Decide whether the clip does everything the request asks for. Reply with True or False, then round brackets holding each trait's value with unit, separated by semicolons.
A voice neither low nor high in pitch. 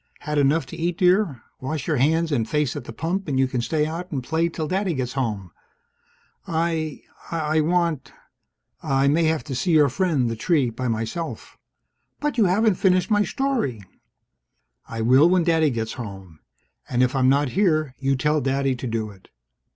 True (150 Hz)